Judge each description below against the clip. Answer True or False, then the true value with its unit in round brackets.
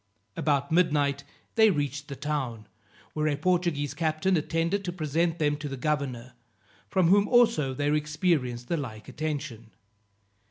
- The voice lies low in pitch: False (150 Hz)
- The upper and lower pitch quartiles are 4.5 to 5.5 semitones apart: False (3.2 semitones)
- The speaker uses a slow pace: False (145 wpm)